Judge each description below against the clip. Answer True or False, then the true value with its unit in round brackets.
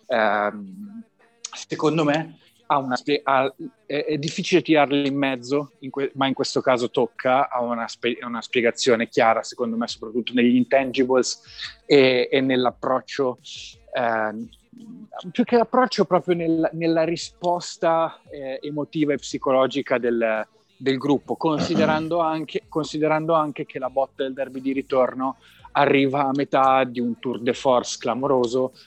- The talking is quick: False (135 wpm)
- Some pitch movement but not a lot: True (3.8 semitones)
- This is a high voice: False (135 Hz)